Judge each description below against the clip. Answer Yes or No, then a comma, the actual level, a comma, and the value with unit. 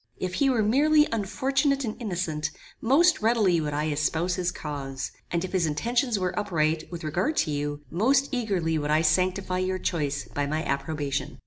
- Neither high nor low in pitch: Yes, medium, 180 Hz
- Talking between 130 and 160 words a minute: No, average, 180 wpm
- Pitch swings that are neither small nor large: No, wide, 6.7 semitones